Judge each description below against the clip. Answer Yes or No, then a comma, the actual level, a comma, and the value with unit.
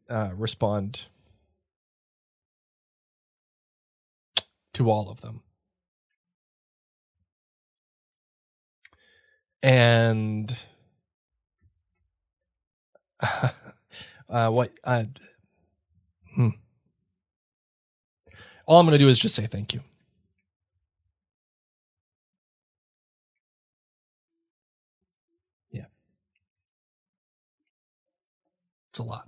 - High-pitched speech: No, low, 100 Hz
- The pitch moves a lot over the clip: Yes, wide, 5.8 semitones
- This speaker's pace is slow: Yes, slow, 50 wpm